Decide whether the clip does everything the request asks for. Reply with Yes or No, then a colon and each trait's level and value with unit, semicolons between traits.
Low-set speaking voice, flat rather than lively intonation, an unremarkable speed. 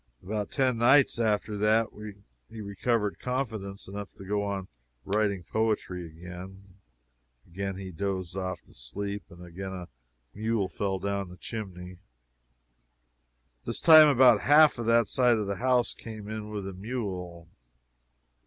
No: low, 100 Hz; average, 3.2 semitones; average, 145 wpm